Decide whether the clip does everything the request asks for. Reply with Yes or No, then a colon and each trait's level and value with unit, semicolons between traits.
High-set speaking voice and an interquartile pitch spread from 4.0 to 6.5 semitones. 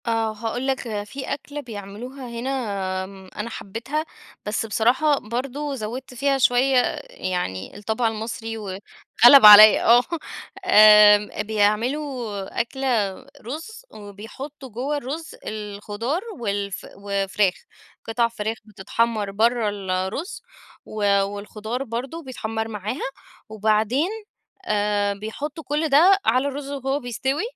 Yes: high, 225 Hz; average, 4.4 semitones